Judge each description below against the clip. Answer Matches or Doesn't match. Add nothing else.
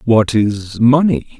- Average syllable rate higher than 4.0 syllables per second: Doesn't match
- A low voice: Matches